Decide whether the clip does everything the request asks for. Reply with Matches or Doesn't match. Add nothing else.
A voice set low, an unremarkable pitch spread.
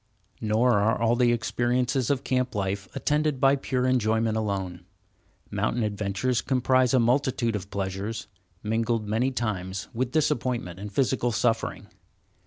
Matches